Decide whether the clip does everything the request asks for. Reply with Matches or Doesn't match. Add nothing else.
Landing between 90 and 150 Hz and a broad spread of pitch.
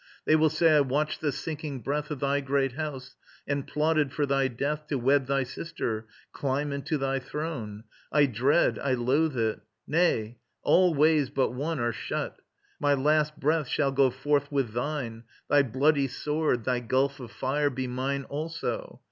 Doesn't match